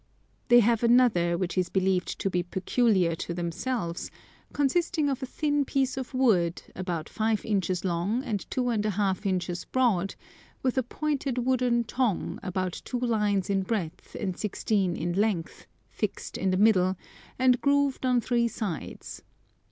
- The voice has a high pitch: Yes, high, 215 Hz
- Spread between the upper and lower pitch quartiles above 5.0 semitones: Yes, wide, 5.4 semitones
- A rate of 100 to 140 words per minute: No, average, 160 wpm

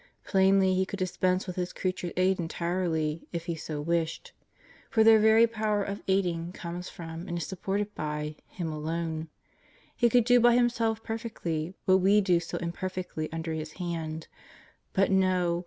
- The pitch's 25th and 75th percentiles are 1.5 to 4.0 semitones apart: Yes, average, 3.2 semitones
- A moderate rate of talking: Yes, average, 170 wpm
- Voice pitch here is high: No, medium, 180 Hz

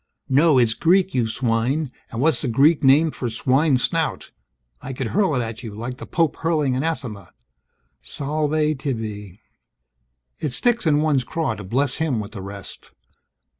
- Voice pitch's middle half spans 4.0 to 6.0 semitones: Yes, average, 5.2 semitones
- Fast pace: No, average, 165 wpm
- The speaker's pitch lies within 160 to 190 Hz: No, low, 135 Hz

